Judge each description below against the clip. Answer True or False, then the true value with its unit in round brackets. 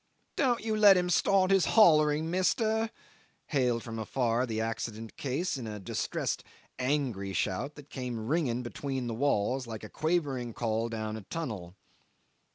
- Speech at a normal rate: True (155 wpm)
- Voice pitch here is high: False (130 Hz)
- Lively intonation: True (6.6 semitones)